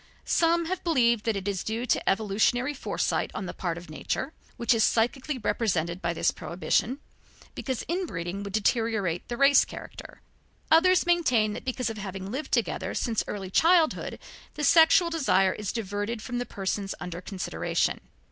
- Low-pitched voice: No, high, 225 Hz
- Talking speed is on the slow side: No, average, 165 wpm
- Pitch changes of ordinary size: No, wide, 6.1 semitones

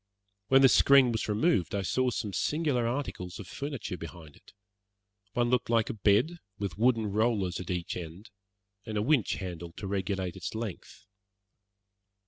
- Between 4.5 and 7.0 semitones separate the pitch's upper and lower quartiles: Yes, average, 5.0 semitones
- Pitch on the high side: No, low, 105 Hz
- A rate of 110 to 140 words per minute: No, average, 160 wpm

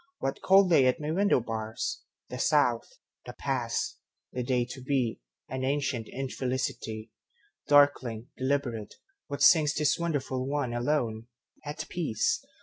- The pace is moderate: No, slow, 115 wpm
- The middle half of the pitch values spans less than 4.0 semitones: Yes, average, 3.5 semitones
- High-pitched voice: No, low, 130 Hz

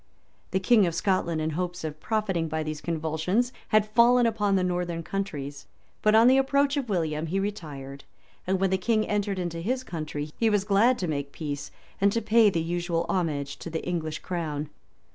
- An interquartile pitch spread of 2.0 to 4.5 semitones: No, average, 5.1 semitones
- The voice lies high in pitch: No, medium, 180 Hz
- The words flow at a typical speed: Yes, average, 190 wpm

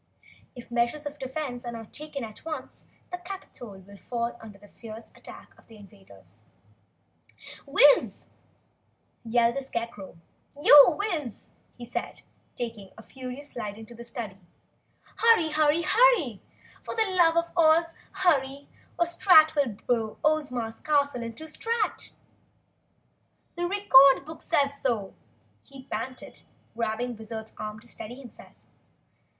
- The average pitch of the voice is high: Yes, very high, 255 Hz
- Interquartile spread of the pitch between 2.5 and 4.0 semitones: No, wide, 5.5 semitones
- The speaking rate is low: Yes, slow, 130 wpm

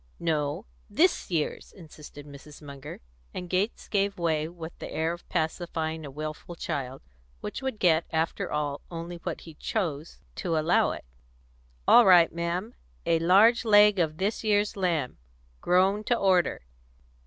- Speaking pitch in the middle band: Yes, medium, 170 Hz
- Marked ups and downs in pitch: No, average, 4.0 semitones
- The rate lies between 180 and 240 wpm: No, average, 150 wpm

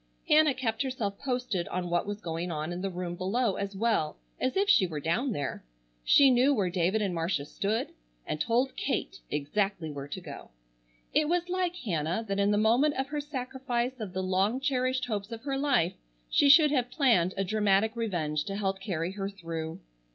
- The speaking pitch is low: No, high, 210 Hz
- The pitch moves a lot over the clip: Yes, wide, 6.3 semitones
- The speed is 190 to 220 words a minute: Yes, average, 195 wpm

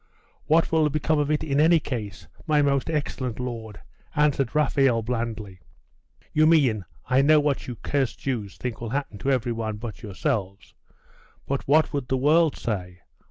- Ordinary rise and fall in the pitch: Yes, average, 4.8 semitones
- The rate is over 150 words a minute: Yes, average, 165 wpm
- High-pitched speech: No, low, 130 Hz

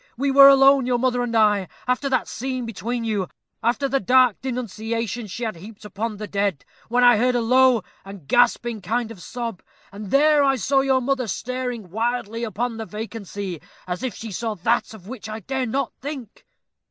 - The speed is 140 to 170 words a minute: No, average, 190 wpm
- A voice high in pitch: Yes, high, 235 Hz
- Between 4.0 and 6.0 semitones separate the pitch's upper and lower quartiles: No, average, 3.3 semitones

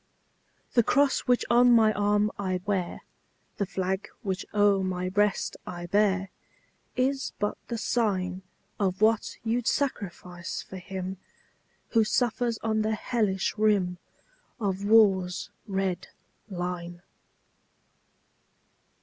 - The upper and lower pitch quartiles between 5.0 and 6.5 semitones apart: No, average, 3.0 semitones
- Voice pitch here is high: Yes, high, 200 Hz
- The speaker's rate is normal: No, slow, 115 wpm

